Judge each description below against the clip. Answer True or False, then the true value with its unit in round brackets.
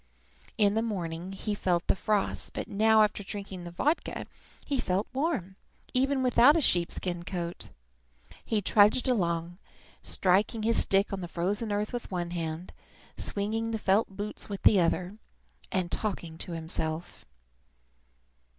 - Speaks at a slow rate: False (150 wpm)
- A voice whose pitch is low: False (195 Hz)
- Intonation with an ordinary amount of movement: True (3.9 semitones)